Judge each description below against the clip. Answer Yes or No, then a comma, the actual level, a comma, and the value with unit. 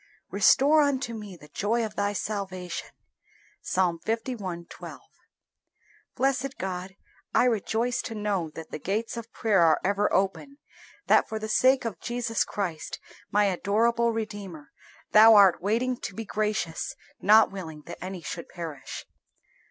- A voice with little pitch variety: No, average, 3.8 semitones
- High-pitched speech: Yes, high, 205 Hz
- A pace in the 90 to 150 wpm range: Yes, average, 145 wpm